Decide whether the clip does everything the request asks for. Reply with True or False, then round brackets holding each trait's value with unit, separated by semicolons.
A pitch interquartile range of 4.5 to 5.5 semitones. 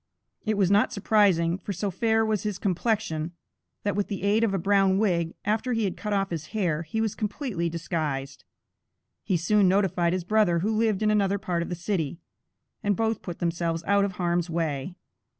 False (3.7 semitones)